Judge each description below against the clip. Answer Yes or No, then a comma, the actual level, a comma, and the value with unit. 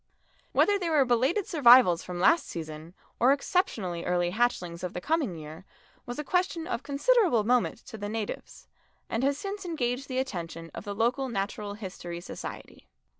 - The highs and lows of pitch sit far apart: Yes, wide, 8.0 semitones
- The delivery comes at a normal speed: Yes, average, 170 wpm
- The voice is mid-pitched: No, high, 235 Hz